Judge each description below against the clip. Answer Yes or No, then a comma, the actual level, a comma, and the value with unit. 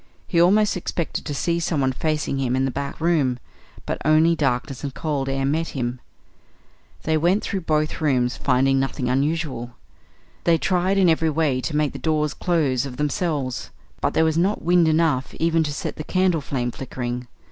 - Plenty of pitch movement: No, average, 3.8 semitones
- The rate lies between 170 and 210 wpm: Yes, average, 180 wpm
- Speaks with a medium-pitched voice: Yes, medium, 150 Hz